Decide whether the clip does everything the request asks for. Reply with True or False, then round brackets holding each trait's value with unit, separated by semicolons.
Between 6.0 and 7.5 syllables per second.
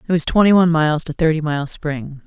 True (6.2 syllables/s)